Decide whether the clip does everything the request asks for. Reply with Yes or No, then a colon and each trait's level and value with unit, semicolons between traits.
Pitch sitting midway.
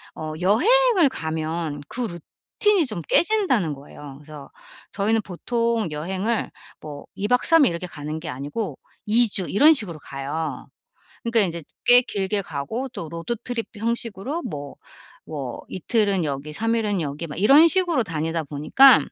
No: high, 195 Hz